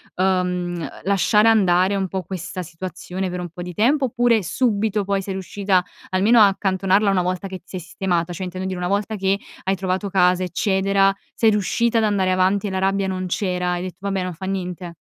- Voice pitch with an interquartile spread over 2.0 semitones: No, narrow, 1.7 semitones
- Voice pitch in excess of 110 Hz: Yes, high, 190 Hz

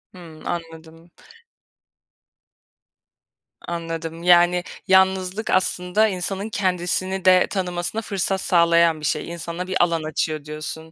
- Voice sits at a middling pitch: Yes, medium, 175 Hz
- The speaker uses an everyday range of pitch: No, narrow, 2.1 semitones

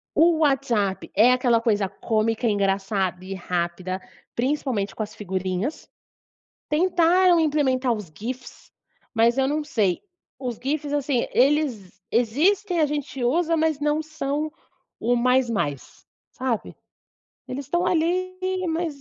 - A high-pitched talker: Yes, very high, 255 Hz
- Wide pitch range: Yes, wide, 6.3 semitones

